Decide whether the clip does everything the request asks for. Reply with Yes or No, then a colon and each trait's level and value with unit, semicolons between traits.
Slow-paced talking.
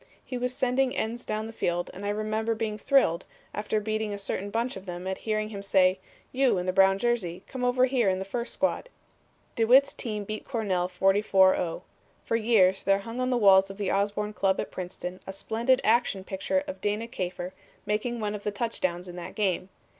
No: fast, 205 wpm